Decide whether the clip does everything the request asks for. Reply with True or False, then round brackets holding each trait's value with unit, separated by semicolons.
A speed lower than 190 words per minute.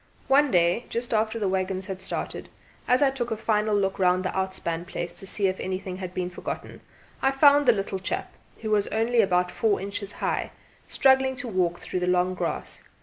False (205 wpm)